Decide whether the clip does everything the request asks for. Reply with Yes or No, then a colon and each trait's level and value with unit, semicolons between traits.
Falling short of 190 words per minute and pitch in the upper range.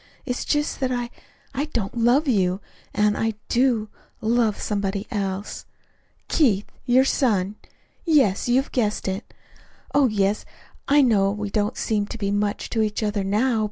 Yes: average, 160 wpm; high, 215 Hz